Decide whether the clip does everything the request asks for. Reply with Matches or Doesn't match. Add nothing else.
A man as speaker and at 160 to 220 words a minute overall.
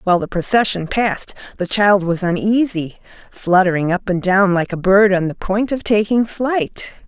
Doesn't match